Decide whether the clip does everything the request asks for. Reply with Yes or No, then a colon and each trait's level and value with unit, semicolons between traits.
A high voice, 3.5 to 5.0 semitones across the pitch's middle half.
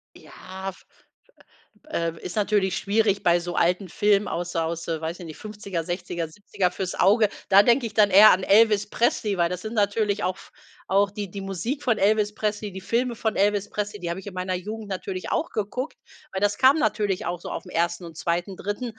No: high, 200 Hz; average, 2.8 semitones